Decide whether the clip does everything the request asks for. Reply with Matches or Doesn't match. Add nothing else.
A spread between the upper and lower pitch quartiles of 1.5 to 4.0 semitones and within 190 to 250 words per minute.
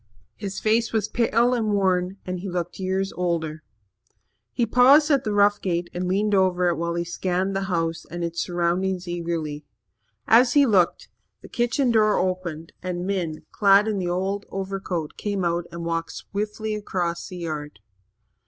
Doesn't match